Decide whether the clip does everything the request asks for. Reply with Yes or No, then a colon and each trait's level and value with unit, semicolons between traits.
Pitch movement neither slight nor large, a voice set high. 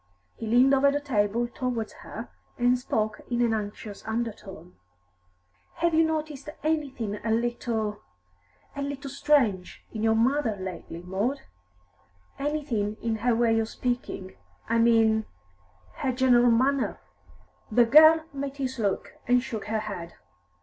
Yes: average, 4.0 semitones; high, 235 Hz